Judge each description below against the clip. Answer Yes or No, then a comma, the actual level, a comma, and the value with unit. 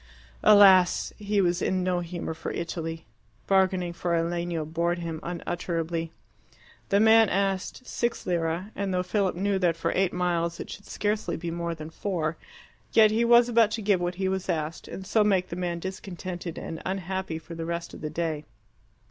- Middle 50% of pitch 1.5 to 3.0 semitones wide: Yes, narrow, 2.5 semitones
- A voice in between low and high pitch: Yes, medium, 180 Hz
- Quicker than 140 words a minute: Yes, average, 185 wpm